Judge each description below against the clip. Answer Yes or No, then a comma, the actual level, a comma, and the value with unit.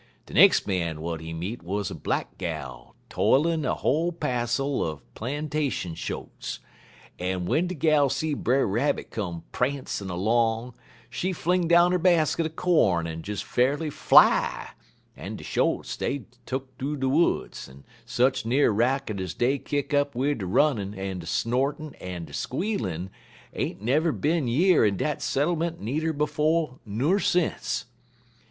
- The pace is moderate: Yes, average, 155 wpm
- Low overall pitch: Yes, low, 130 Hz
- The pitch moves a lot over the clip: Yes, wide, 7.8 semitones